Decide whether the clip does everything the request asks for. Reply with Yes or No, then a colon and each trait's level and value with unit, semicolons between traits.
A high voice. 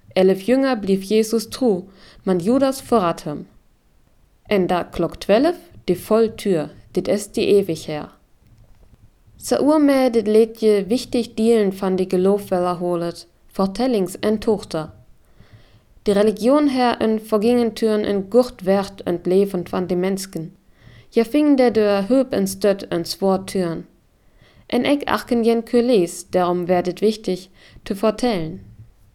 Yes: high, 200 Hz